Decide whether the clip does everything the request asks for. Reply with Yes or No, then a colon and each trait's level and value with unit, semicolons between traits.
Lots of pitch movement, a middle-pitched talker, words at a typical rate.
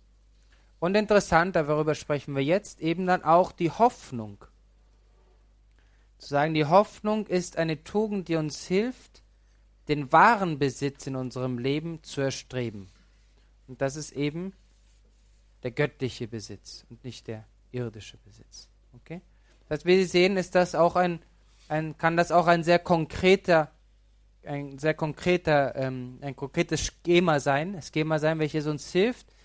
Yes: wide, 6.6 semitones; medium, 150 Hz; average, 145 wpm